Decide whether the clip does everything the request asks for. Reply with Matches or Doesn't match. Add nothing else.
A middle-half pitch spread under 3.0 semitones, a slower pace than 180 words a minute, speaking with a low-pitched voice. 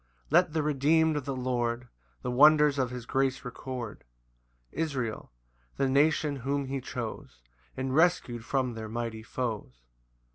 Doesn't match